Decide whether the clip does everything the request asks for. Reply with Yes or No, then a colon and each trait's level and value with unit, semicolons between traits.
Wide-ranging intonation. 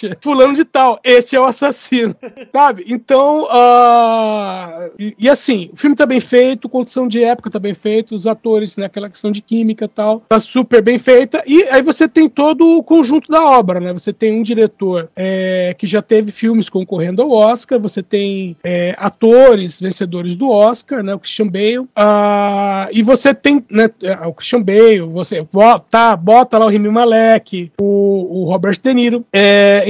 No: average, 3.9 semitones